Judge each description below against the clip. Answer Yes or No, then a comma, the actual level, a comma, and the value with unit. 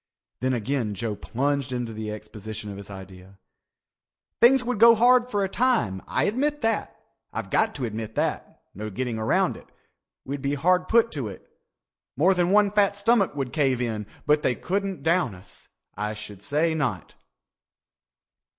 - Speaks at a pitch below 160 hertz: Yes, medium, 140 Hz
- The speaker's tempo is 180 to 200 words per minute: No, average, 170 wpm